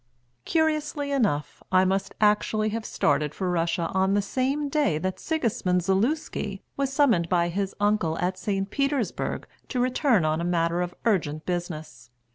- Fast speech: No, average, 155 wpm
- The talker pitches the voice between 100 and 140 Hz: No, high, 195 Hz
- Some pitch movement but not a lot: No, wide, 6.5 semitones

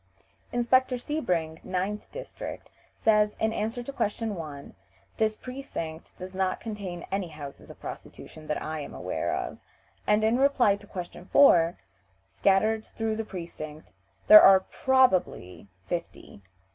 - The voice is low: No, high, 200 Hz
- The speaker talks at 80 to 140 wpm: Yes, slow, 135 wpm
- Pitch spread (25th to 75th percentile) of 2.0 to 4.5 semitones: No, average, 4.9 semitones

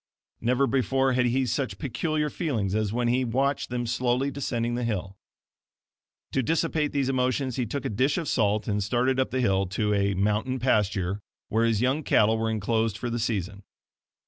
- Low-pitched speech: Yes, low, 120 Hz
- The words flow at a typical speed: Yes, average, 185 wpm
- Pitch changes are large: No, average, 3.7 semitones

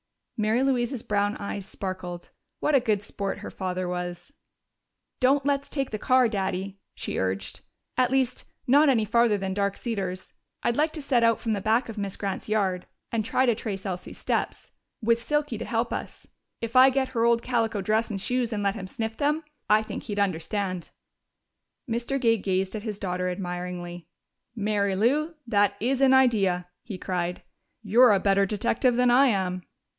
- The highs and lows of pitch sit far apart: No, average, 4.2 semitones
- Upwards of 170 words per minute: Yes, average, 180 wpm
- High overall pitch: Yes, high, 215 Hz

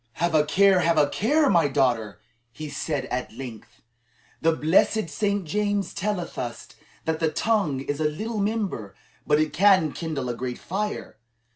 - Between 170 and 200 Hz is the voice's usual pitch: No, medium, 160 Hz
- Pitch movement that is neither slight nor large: No, wide, 6.5 semitones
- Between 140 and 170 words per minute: Yes, average, 165 wpm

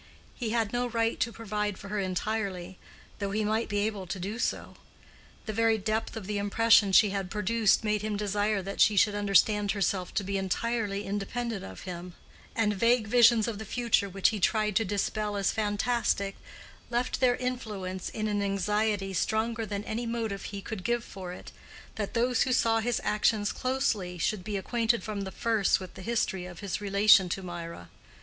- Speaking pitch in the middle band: No, high, 210 Hz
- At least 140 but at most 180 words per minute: No, average, 190 wpm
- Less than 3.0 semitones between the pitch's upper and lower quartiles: Yes, narrow, 2.4 semitones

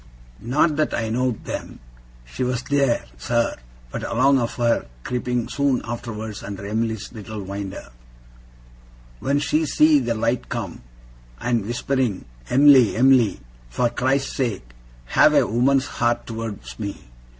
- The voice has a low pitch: Yes, low, 120 Hz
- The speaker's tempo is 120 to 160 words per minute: Yes, slow, 135 wpm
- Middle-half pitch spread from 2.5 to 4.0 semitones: Yes, average, 3.2 semitones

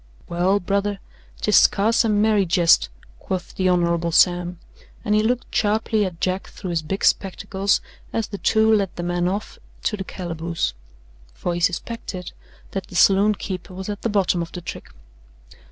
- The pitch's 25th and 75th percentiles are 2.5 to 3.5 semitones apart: Yes, average, 2.8 semitones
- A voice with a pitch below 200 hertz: Yes, high, 190 Hz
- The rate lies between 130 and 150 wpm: No, average, 170 wpm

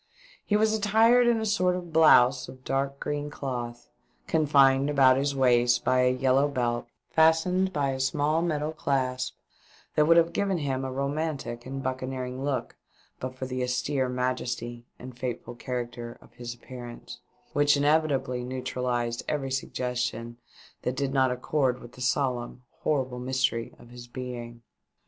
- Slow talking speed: No, average, 155 wpm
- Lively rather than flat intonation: No, average, 2.8 semitones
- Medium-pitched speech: No, low, 130 Hz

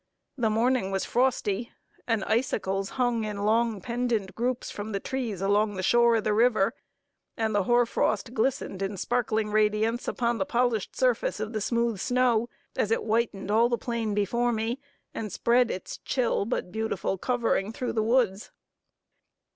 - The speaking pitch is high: Yes, high, 225 Hz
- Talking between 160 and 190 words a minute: Yes, average, 165 wpm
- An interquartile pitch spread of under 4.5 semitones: Yes, narrow, 2.5 semitones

